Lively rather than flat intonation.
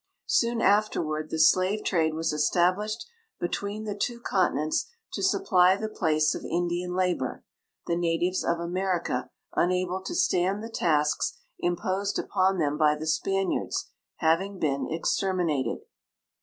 No: average, 3.3 semitones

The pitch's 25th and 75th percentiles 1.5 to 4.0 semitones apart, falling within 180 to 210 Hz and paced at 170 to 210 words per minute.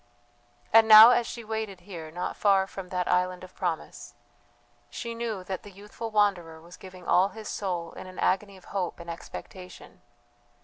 Yes: average, 2.7 semitones; high, 190 Hz; average, 175 wpm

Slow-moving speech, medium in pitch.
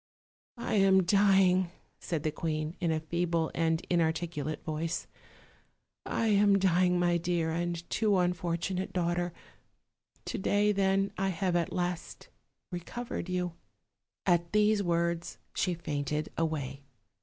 Yes: slow, 130 wpm; medium, 175 Hz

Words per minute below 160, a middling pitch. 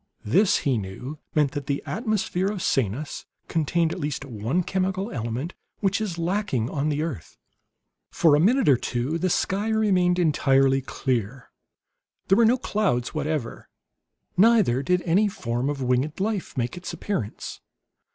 Yes: average, 150 wpm; medium, 155 Hz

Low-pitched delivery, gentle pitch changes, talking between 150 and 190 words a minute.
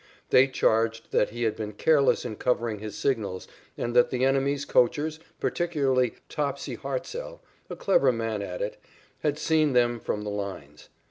No: low, 125 Hz; average, 4.7 semitones; average, 160 wpm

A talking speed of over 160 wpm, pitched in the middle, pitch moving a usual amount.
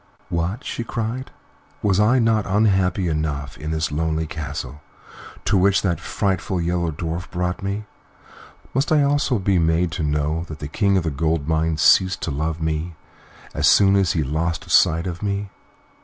No: average, 170 wpm; very low, 85 Hz; average, 3.9 semitones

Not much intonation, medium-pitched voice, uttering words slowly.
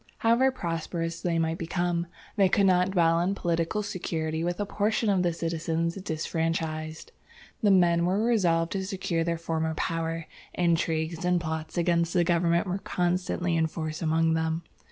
No: narrow, 1.9 semitones; medium, 170 Hz; average, 160 wpm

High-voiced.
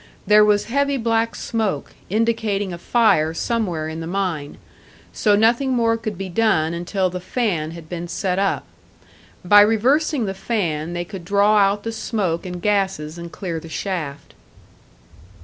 Yes: high, 195 Hz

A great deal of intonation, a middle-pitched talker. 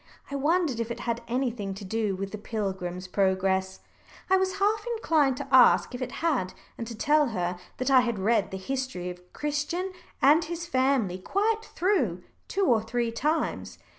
No: wide, 7.6 semitones; high, 240 Hz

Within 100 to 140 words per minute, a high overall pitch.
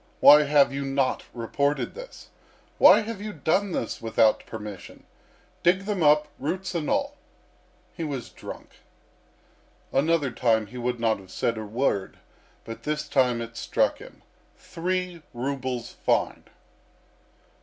No: slow, 135 wpm; medium, 140 Hz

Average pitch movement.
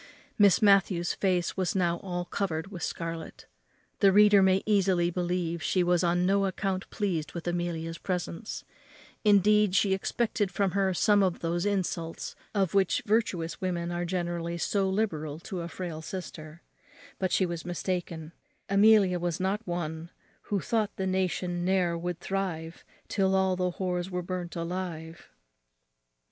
No: narrow, 2.1 semitones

